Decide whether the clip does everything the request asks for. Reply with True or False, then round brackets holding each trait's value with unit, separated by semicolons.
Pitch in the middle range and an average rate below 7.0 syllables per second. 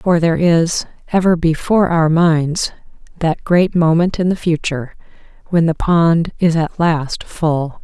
True (165 Hz; 4.2 syllables/s)